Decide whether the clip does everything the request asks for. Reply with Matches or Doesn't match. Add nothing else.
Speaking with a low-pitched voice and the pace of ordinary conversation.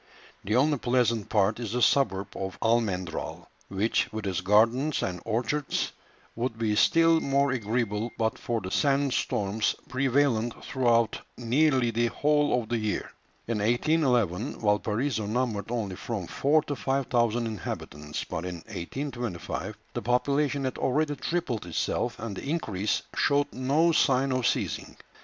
Matches